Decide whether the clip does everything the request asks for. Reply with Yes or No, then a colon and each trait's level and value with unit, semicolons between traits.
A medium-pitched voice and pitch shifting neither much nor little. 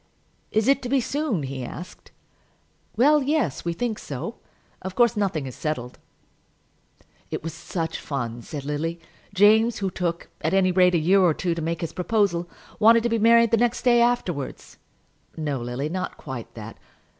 No: medium, 180 Hz; wide, 6.9 semitones